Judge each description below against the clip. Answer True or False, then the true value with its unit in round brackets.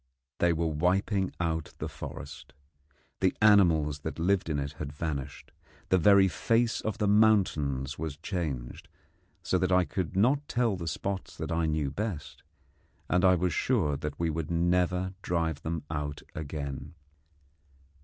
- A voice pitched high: False (85 Hz)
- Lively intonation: False (4.0 semitones)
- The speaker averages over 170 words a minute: False (155 wpm)